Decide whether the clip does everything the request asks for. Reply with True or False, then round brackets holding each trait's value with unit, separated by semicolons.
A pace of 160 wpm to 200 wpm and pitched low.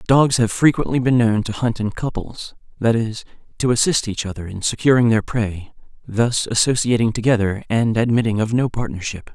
True (175 wpm; 115 Hz)